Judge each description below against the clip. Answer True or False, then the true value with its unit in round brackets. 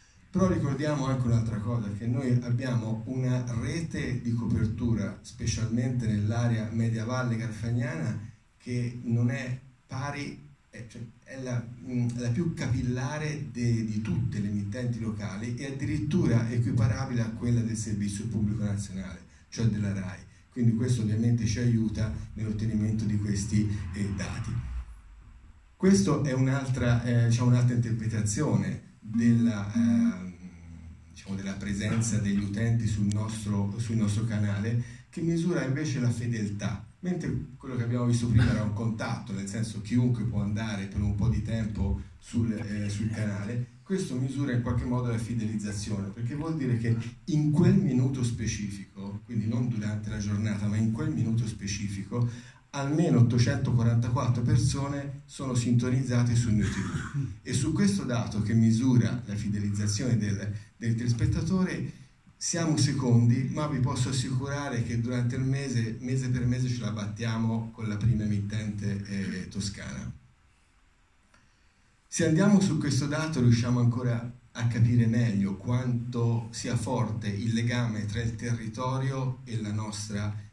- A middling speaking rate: True (140 wpm)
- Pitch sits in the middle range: False (115 Hz)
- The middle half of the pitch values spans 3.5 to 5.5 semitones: False (2.8 semitones)